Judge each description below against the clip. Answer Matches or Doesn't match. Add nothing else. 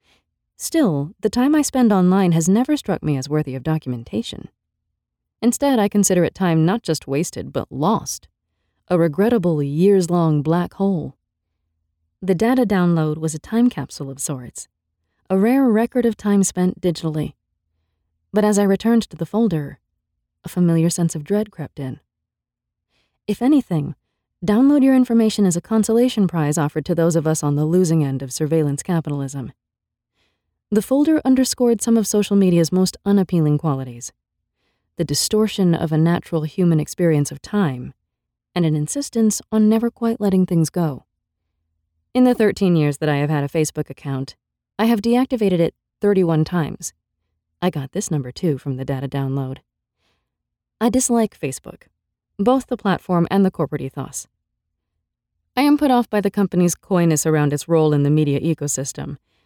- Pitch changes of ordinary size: Doesn't match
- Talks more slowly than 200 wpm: Matches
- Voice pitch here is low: Doesn't match